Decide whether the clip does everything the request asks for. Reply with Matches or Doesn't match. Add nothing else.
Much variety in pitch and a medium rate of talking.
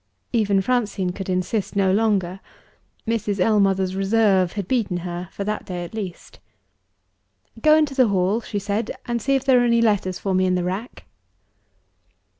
Doesn't match